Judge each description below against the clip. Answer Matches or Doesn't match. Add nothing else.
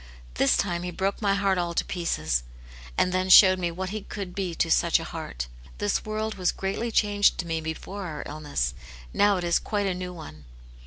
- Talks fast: Matches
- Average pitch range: Matches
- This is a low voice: Doesn't match